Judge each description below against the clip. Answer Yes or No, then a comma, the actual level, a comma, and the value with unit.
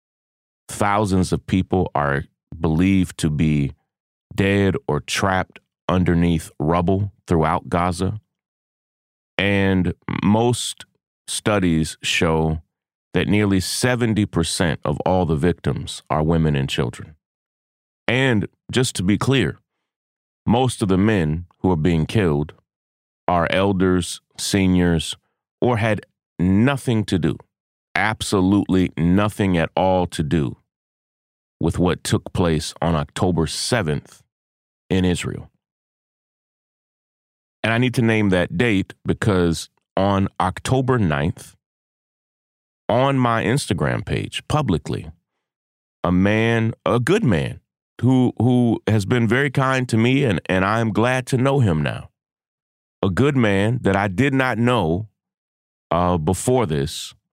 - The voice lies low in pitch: Yes, very low, 95 Hz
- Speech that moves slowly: Yes, slow, 120 wpm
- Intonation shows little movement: No, average, 5.3 semitones